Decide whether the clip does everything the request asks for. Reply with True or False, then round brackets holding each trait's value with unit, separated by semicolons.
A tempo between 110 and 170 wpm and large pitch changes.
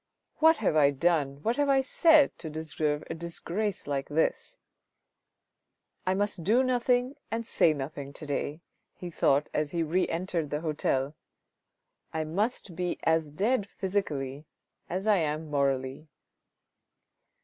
True (155 wpm; 5.7 semitones)